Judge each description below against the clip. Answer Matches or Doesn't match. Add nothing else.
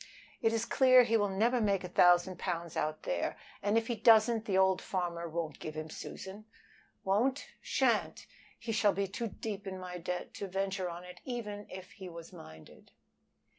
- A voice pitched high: Matches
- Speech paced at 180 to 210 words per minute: Matches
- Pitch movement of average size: Matches